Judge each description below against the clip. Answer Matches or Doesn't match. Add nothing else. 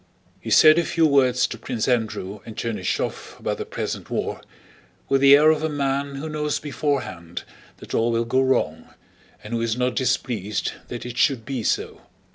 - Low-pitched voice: Matches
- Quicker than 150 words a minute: Matches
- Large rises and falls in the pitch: Doesn't match